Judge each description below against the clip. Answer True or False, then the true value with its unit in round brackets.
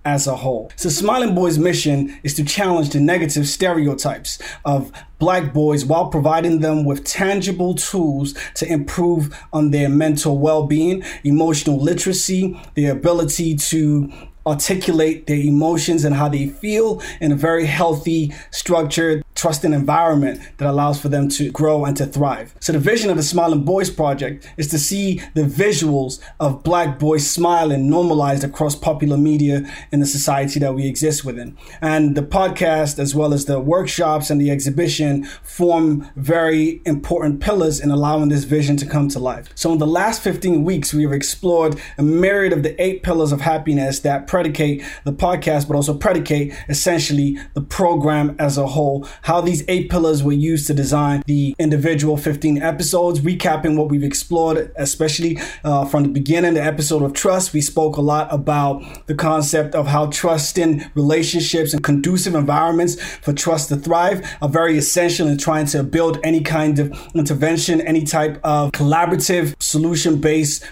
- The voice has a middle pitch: True (155 Hz)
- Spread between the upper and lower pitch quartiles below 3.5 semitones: True (2.4 semitones)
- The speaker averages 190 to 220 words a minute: False (170 wpm)